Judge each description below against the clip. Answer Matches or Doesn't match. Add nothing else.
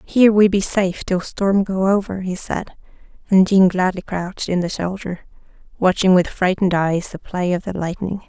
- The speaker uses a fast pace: Doesn't match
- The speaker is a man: Doesn't match